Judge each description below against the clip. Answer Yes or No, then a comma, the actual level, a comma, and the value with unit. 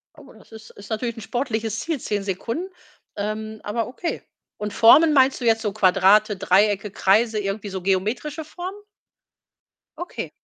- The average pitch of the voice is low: No, high, 220 Hz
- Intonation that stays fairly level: No, average, 3.4 semitones